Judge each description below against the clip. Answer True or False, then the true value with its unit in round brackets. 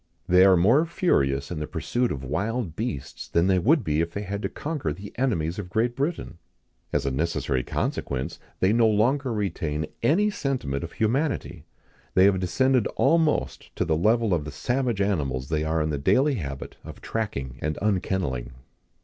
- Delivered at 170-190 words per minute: True (180 wpm)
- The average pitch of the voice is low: True (95 Hz)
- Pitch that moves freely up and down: True (7.8 semitones)